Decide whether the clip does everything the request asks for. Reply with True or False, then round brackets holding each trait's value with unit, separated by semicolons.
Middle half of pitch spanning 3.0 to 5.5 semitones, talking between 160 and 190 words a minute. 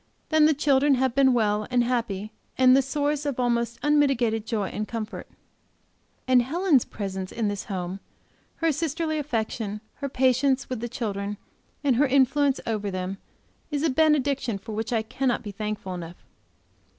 True (4.7 semitones; 165 wpm)